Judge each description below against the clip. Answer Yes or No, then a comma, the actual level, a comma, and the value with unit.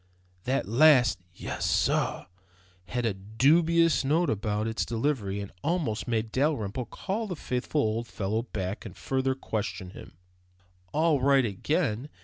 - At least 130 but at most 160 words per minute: Yes, slow, 135 wpm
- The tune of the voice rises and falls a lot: Yes, wide, 5.7 semitones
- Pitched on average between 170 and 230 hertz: No, low, 125 Hz